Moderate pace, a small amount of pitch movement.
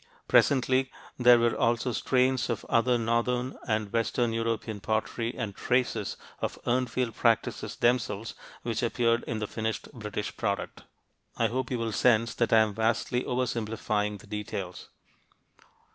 Yes: average, 145 wpm; narrow, 2.1 semitones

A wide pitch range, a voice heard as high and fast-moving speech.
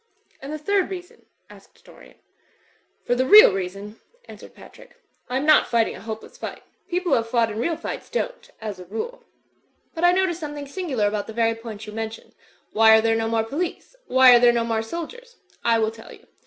Yes: wide, 7.2 semitones; high, 235 Hz; fast, 210 wpm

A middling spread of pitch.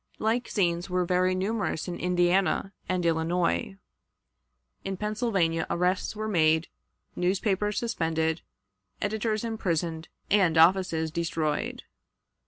Yes: average, 3.7 semitones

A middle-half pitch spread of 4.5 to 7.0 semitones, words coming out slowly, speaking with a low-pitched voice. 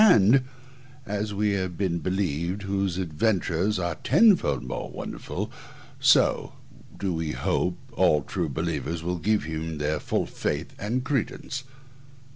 No: average, 4.1 semitones; slow, 130 wpm; very low, 95 Hz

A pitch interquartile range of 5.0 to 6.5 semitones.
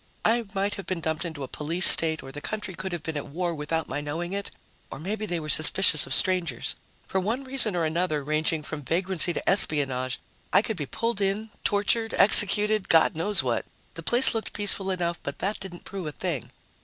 No: average, 4.4 semitones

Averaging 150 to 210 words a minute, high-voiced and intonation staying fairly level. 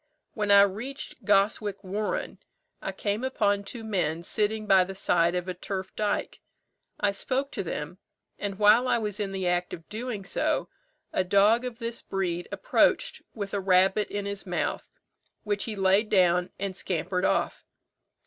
Yes: average, 165 wpm; high, 200 Hz; narrow, 2.3 semitones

